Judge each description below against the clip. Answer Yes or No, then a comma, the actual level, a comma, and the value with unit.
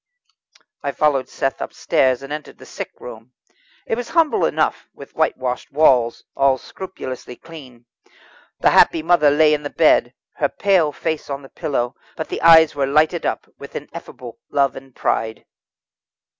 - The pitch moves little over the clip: No, average, 3.5 semitones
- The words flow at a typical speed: Yes, average, 155 wpm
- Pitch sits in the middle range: Yes, medium, 145 Hz